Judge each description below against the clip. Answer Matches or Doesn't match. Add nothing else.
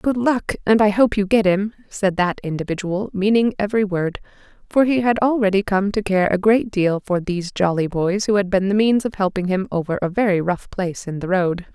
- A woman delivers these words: Matches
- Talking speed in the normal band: Doesn't match